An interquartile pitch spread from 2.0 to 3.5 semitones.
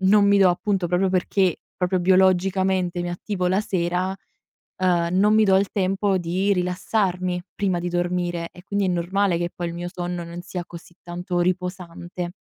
No: narrow, 1.5 semitones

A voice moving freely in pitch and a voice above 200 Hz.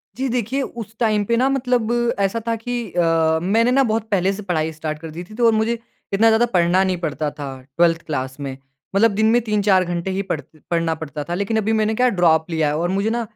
No: wide, 5.7 semitones; high, 195 Hz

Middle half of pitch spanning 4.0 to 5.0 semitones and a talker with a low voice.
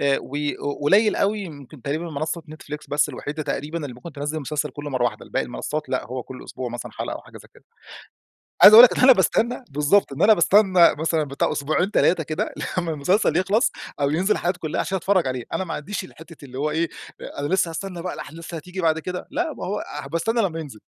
No: average, 4.7 semitones; medium, 160 Hz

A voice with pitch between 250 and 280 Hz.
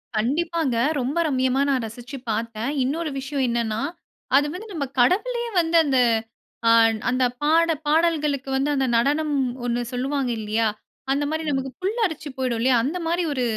Yes: very high, 275 Hz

